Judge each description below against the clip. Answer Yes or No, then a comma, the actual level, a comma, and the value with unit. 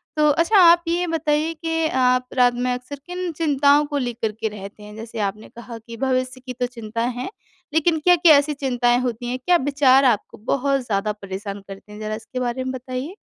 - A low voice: No, very high, 255 Hz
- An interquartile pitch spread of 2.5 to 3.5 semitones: No, average, 4.5 semitones